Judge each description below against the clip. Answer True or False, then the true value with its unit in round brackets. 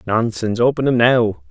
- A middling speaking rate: True (160 wpm)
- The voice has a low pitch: True (115 Hz)